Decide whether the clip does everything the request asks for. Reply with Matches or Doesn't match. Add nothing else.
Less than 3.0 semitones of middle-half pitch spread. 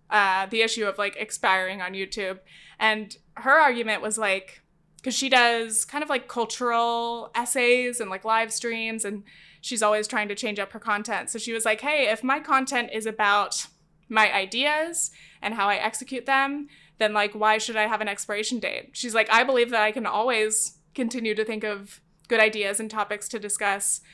Matches